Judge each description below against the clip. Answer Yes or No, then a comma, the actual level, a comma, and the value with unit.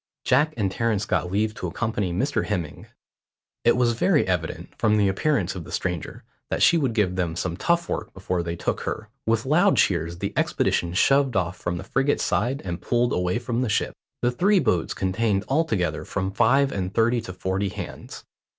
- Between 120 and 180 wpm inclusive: No, average, 195 wpm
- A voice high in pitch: No, low, 105 Hz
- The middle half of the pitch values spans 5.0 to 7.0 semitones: Yes, average, 5.3 semitones